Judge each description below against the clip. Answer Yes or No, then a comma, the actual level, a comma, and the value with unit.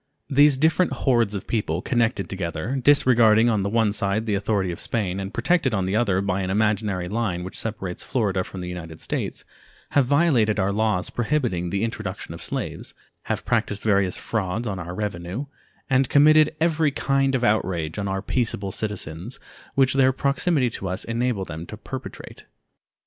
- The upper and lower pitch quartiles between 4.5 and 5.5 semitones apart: Yes, average, 5.1 semitones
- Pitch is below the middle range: Yes, low, 105 Hz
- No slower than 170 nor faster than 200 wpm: Yes, average, 175 wpm